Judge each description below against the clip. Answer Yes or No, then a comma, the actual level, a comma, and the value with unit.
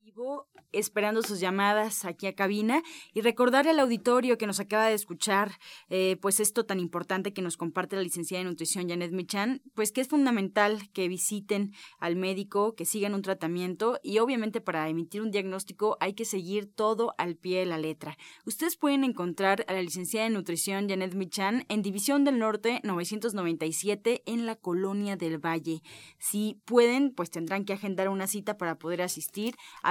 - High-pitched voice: Yes, high, 200 Hz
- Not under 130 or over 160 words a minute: No, average, 175 wpm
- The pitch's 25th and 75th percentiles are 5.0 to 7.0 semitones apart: No, average, 3.5 semitones